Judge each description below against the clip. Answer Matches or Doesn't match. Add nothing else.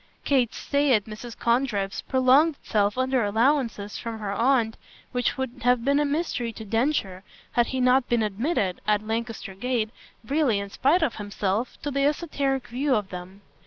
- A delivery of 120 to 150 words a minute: Doesn't match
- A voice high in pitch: Matches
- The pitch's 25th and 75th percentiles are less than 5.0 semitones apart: Matches